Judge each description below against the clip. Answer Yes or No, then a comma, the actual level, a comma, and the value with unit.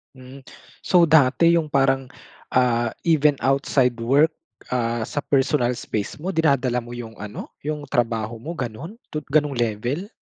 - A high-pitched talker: No, low, 135 Hz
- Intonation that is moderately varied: Yes, average, 4.0 semitones